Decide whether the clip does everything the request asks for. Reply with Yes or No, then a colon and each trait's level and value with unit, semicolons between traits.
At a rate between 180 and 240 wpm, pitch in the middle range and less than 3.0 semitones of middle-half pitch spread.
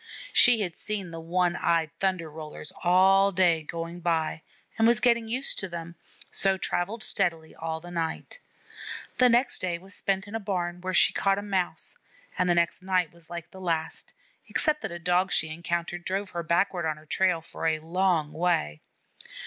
Yes: average, 190 wpm; medium, 175 Hz; narrow, 2.6 semitones